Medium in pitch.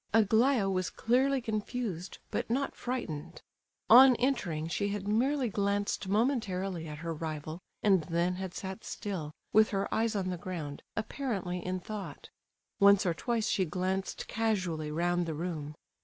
No: high, 195 Hz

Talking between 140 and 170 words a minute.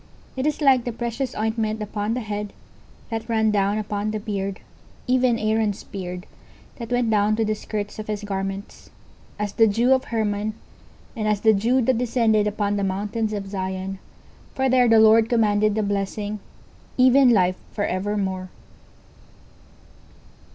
Yes: average, 165 wpm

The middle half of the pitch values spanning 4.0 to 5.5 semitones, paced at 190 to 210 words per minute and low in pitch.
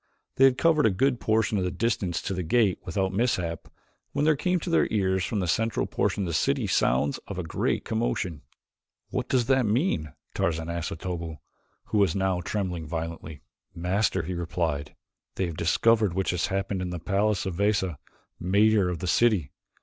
Yes: average, 4.4 semitones; average, 195 wpm; very low, 95 Hz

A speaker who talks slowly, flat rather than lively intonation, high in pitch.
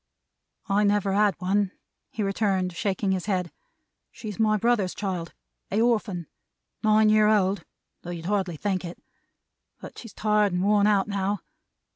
No: average, 150 wpm; narrow, 2.1 semitones; high, 200 Hz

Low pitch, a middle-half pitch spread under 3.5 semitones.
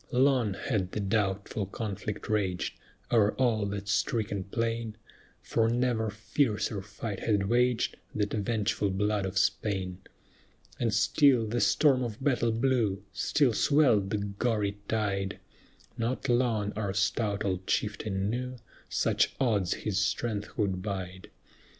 Yes: low, 105 Hz; average, 2.9 semitones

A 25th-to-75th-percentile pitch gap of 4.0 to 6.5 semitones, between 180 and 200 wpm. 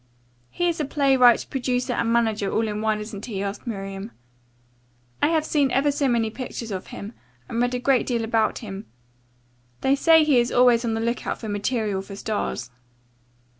No: average, 3.6 semitones; average, 185 wpm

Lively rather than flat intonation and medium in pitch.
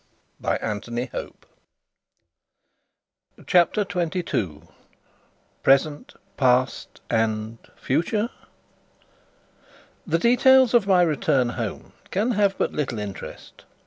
Yes: wide, 9.0 semitones; medium, 150 Hz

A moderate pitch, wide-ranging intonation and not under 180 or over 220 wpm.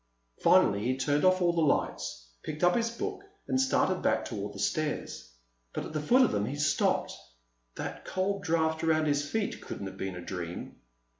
Yes: medium, 155 Hz; wide, 6.5 semitones; average, 195 wpm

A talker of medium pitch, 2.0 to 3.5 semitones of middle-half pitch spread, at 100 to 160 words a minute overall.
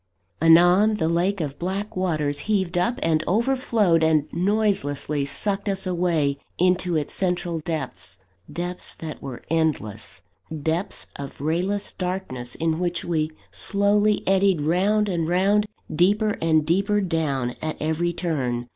No: medium, 175 Hz; average, 3.9 semitones; slow, 135 wpm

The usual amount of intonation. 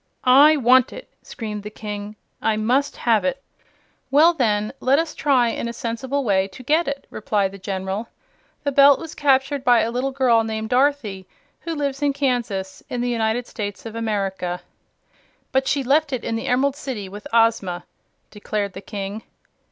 Yes: average, 4.7 semitones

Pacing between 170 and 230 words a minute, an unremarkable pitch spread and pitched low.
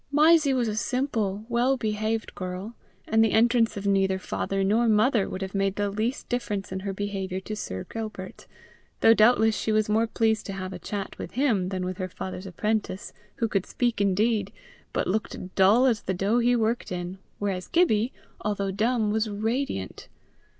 No: average, 185 wpm; average, 3.0 semitones; high, 210 Hz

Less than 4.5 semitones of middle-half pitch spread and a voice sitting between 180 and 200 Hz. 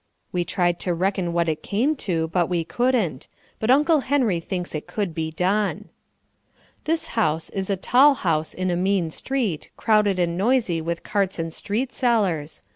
No: average, 4.8 semitones; medium, 185 Hz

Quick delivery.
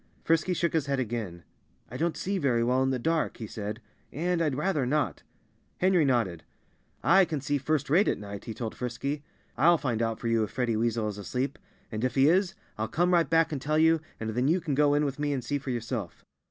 Yes: fast, 235 wpm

